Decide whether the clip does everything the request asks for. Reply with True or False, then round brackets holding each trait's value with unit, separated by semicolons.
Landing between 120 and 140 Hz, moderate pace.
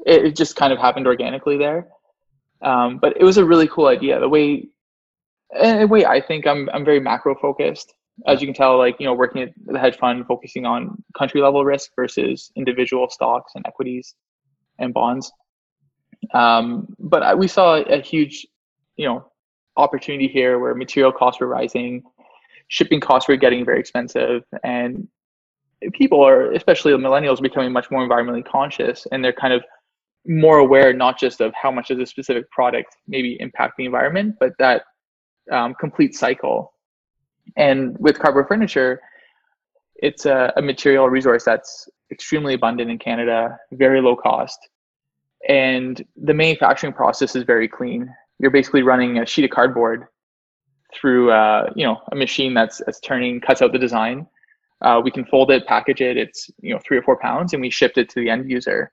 True (135 Hz; 175 wpm)